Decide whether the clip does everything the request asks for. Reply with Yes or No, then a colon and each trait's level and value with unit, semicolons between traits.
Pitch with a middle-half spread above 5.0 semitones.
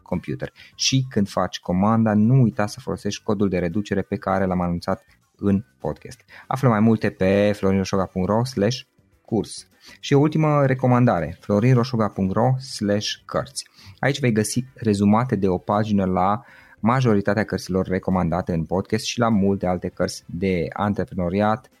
No: average, 3.1 semitones